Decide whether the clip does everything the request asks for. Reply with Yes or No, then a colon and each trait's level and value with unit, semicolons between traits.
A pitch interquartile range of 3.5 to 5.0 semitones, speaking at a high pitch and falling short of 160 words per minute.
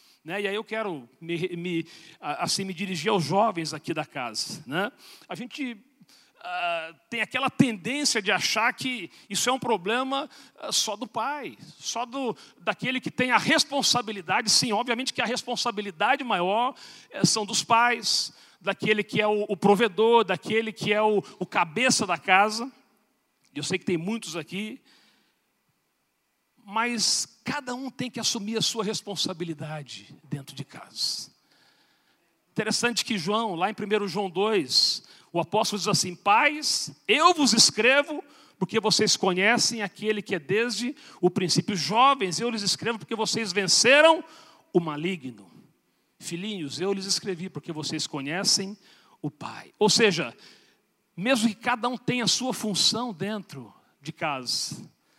Yes: average, 4.5 semitones; high, 210 Hz; average, 150 wpm